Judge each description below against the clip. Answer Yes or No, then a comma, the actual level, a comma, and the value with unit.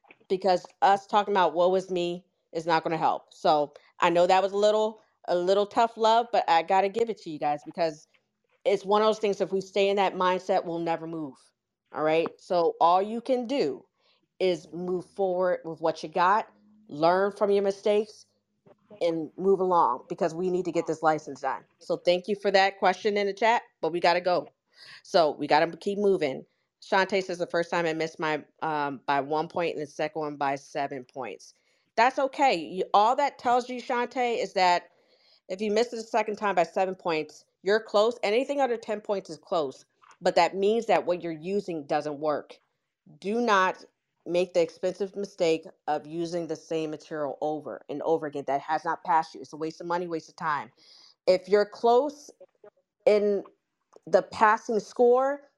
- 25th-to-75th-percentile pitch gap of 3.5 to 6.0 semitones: Yes, average, 4.4 semitones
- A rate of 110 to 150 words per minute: No, average, 200 wpm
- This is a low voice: No, medium, 185 Hz